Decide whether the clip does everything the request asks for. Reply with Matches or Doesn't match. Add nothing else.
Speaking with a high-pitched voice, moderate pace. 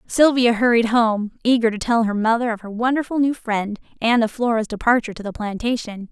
Matches